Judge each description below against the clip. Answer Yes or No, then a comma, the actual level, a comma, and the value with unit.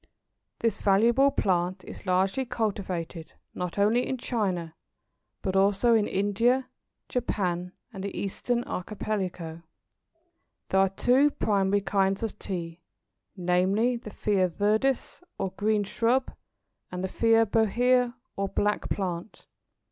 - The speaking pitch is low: No, high, 200 Hz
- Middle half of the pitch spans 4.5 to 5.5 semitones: No, average, 3.6 semitones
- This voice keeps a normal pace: No, slow, 120 wpm